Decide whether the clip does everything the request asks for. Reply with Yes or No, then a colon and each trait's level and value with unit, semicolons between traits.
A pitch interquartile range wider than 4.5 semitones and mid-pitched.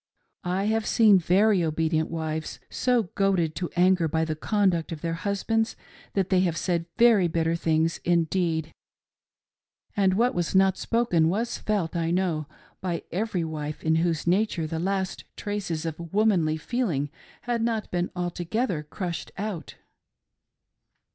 No: average, 3.8 semitones; medium, 175 Hz